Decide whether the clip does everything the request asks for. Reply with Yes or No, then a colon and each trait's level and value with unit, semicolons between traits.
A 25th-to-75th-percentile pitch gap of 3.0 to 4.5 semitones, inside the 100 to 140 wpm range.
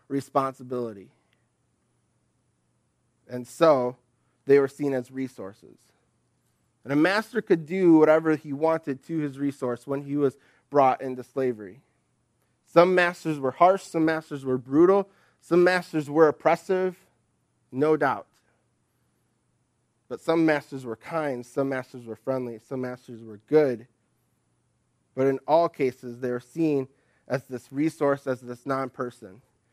Yes: average, 3.9 semitones; slow, 135 wpm